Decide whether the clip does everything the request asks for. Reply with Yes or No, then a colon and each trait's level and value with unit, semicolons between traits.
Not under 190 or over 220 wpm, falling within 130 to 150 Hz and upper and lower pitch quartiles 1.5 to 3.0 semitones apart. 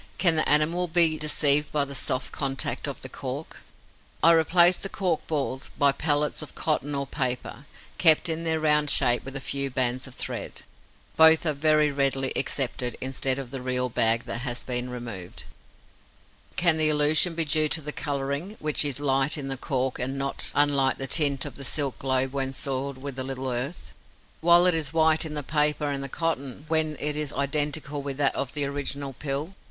Yes: average, 195 wpm; medium, 140 Hz; narrow, 2.5 semitones